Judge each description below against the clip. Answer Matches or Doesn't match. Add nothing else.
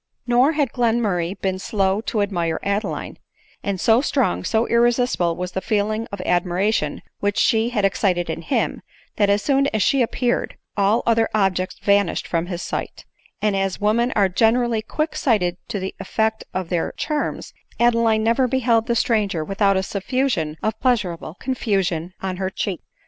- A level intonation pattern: Doesn't match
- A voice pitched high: Matches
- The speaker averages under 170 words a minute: Doesn't match